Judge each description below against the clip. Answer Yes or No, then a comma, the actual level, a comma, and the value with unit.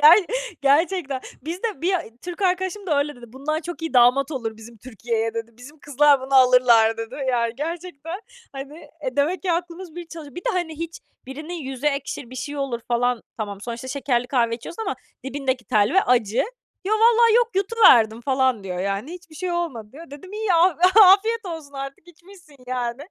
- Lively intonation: Yes, wide, 6.1 semitones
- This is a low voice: No, very high, 285 Hz